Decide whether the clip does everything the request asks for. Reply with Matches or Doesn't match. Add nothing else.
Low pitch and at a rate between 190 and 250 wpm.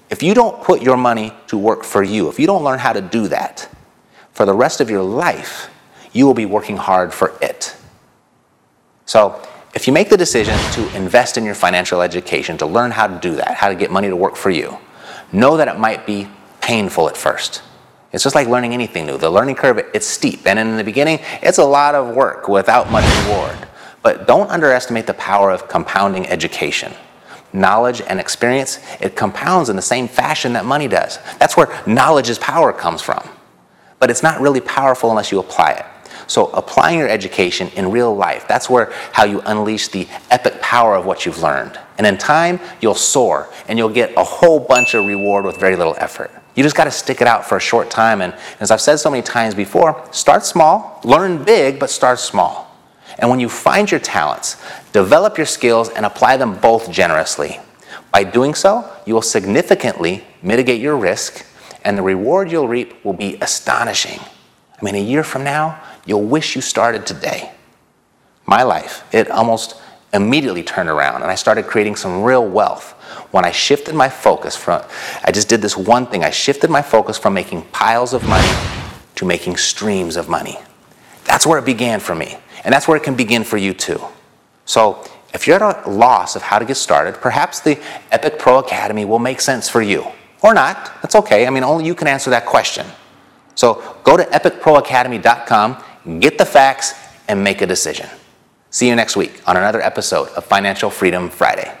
Matches